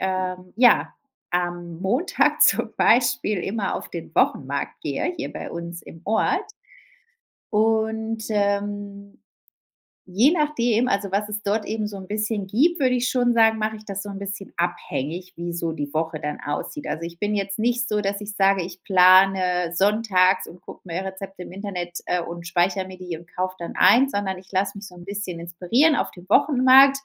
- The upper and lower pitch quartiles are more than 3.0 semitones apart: Yes, average, 3.5 semitones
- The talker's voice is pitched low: No, high, 195 Hz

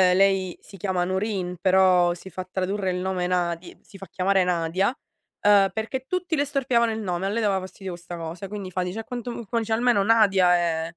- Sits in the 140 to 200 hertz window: Yes, high, 190 Hz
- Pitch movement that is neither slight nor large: Yes, average, 3.2 semitones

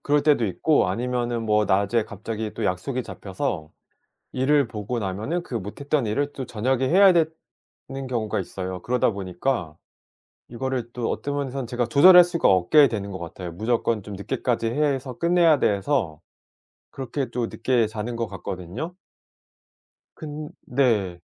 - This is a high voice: No, low, 120 Hz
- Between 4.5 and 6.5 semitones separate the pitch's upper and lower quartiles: Yes, wide, 5.4 semitones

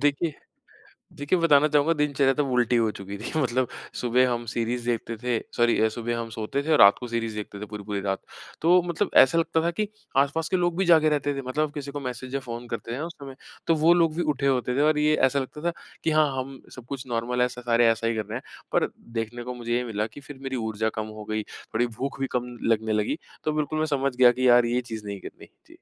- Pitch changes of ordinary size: Yes, average, 4.0 semitones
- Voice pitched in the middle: No, low, 125 Hz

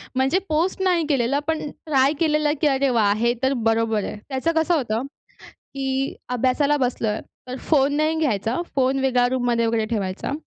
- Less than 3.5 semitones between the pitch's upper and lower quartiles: No, average, 4.2 semitones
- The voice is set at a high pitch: Yes, very high, 265 Hz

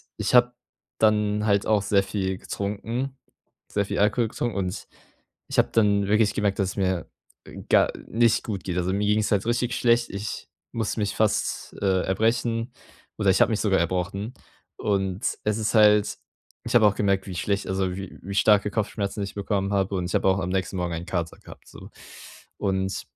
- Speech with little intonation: Yes, narrow, 2.1 semitones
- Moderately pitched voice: No, low, 100 Hz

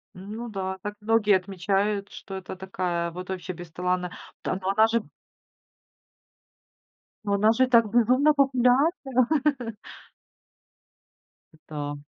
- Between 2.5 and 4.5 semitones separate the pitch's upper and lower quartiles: Yes, average, 4.2 semitones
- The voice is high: Yes, high, 200 Hz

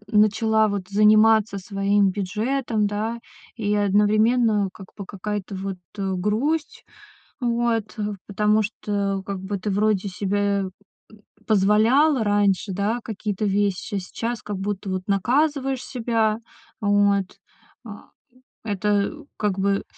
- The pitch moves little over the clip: Yes, narrow, 1.9 semitones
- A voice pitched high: Yes, high, 210 Hz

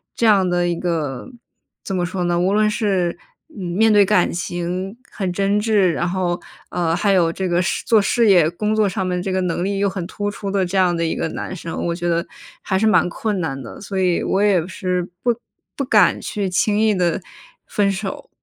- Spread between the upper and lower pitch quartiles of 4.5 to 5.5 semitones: No, average, 2.7 semitones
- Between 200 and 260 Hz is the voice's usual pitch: No, medium, 185 Hz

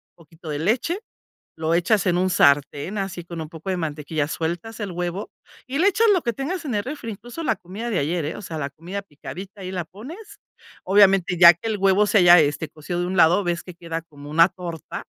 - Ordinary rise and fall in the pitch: Yes, average, 4.2 semitones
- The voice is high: No, medium, 180 Hz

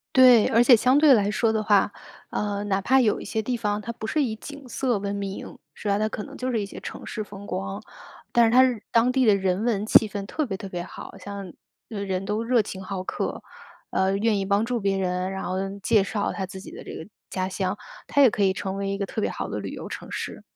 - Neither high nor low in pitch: No, high, 205 Hz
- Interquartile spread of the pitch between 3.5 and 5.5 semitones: No, average, 3.0 semitones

